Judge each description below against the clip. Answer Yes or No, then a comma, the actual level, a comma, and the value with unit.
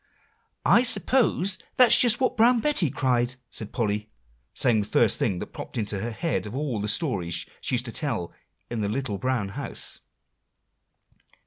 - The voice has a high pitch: No, low, 125 Hz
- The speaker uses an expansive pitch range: Yes, wide, 8.8 semitones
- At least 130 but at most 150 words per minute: No, average, 165 wpm